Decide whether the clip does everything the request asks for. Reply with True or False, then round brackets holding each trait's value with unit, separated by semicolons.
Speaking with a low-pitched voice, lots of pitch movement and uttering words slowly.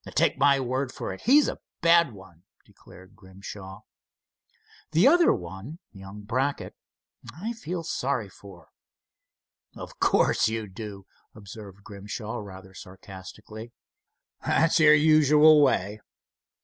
True (110 Hz; 7.7 semitones; 110 wpm)